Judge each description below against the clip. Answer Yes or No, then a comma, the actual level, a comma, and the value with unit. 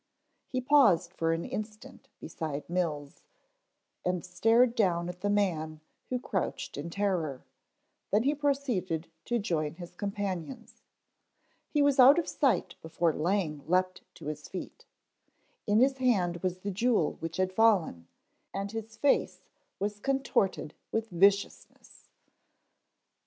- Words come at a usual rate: No, slow, 130 wpm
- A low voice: No, high, 190 Hz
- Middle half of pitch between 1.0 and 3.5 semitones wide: No, average, 5.2 semitones